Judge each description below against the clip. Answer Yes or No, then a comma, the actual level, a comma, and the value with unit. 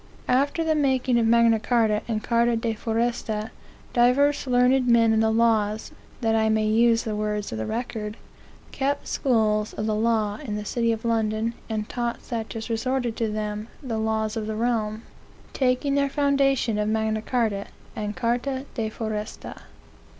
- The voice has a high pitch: Yes, high, 225 Hz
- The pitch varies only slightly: Yes, narrow, 2.1 semitones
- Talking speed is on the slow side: No, average, 170 wpm